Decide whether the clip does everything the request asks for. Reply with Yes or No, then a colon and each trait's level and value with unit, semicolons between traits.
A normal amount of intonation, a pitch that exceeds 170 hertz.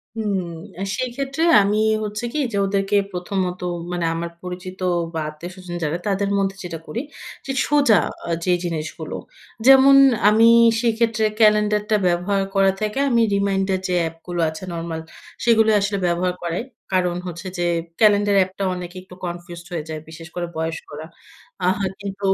Yes: average, 3.3 semitones; high, 190 Hz